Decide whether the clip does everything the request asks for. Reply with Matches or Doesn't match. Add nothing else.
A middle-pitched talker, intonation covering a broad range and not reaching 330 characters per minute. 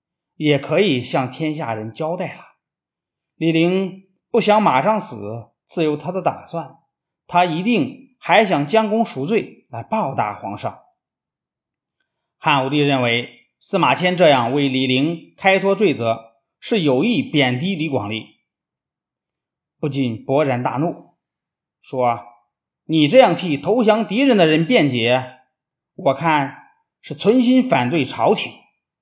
Matches